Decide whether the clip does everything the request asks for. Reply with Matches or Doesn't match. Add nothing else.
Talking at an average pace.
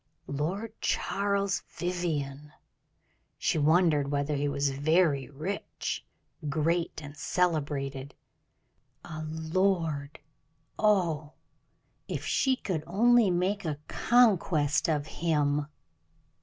Doesn't match